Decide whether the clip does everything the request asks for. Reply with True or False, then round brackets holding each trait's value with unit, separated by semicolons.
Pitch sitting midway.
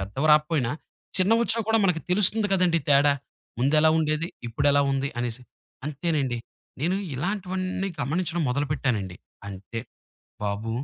True (150 Hz)